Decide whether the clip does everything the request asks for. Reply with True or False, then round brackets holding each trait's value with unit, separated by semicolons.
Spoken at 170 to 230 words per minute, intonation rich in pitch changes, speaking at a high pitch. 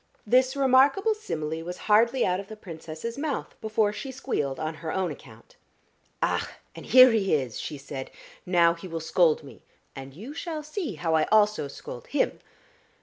True (175 wpm; 8.3 semitones; 195 Hz)